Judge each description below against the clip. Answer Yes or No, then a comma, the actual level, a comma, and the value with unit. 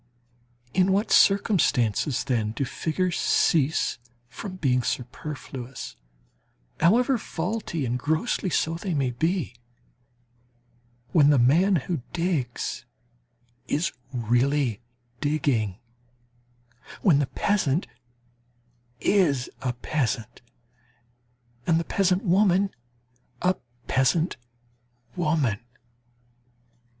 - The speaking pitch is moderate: Yes, medium, 150 Hz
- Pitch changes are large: Yes, wide, 6.3 semitones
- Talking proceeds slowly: Yes, slow, 85 wpm